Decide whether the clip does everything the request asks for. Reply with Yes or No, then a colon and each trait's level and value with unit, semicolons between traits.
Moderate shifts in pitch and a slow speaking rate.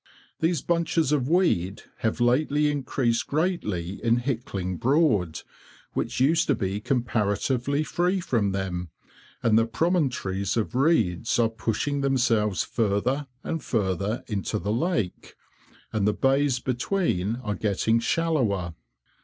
No: wide, 6.0 semitones; slow, 125 wpm